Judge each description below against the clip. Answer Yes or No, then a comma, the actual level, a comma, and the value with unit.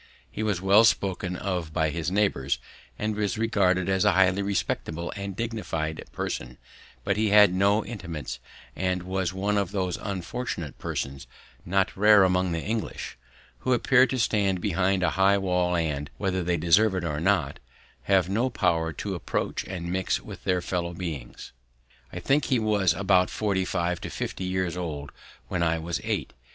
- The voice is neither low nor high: No, very low, 95 Hz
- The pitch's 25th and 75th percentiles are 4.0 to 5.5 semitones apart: No, average, 2.8 semitones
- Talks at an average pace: Yes, average, 170 wpm